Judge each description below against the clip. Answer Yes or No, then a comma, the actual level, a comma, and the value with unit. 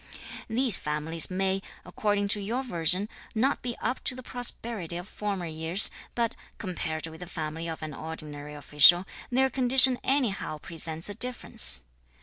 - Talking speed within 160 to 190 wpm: No, average, 150 wpm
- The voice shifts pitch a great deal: Yes, wide, 6.7 semitones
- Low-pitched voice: No, medium, 185 Hz